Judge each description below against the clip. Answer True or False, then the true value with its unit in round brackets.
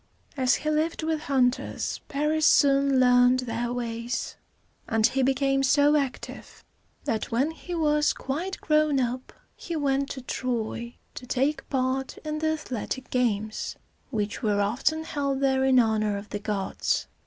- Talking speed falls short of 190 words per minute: True (150 wpm)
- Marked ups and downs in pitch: False (3.5 semitones)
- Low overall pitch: False (265 Hz)